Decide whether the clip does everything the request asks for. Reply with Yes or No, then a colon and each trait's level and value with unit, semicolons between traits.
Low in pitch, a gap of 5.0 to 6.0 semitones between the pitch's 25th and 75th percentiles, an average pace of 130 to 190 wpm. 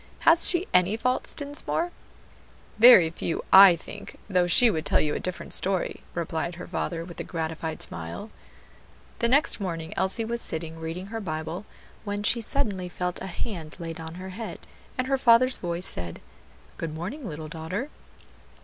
No: medium, 185 Hz; wide, 5.6 semitones; average, 165 wpm